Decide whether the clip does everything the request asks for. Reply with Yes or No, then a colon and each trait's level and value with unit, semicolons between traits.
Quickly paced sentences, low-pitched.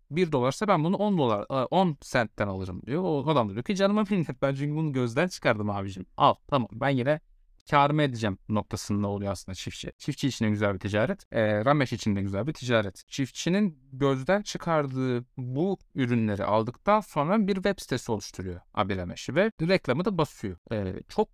Yes: fast, 175 wpm; low, 130 Hz